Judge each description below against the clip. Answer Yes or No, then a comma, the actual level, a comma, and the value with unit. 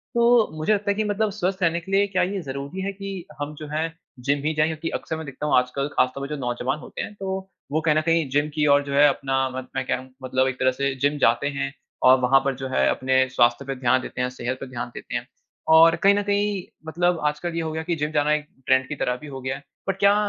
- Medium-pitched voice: Yes, medium, 150 Hz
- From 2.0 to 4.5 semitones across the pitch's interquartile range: No, average, 5.0 semitones